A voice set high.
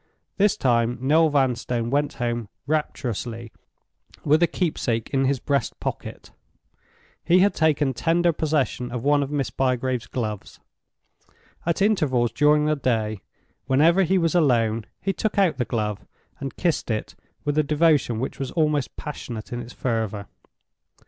No: low, 135 Hz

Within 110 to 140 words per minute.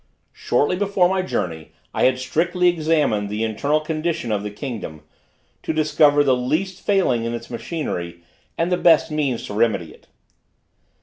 No: average, 160 wpm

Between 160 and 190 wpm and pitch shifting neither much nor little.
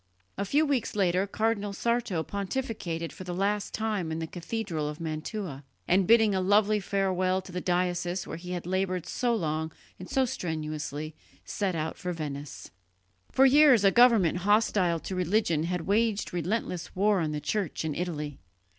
Yes: average, 170 wpm; average, 4.2 semitones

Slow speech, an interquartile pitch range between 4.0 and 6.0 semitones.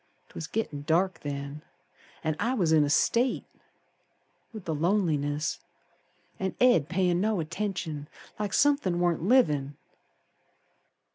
Yes: slow, 120 wpm; wide, 5.5 semitones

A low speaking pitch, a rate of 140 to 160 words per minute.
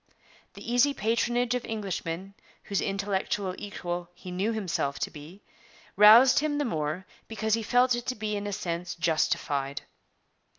No: high, 200 Hz; average, 155 wpm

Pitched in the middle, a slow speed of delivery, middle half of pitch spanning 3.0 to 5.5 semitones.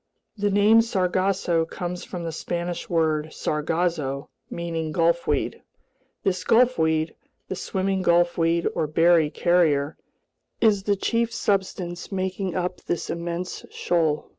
No: medium, 175 Hz; slow, 115 wpm; narrow, 2.6 semitones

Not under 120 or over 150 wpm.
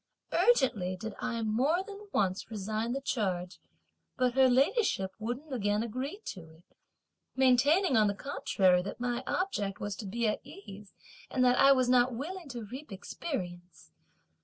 No: average, 160 wpm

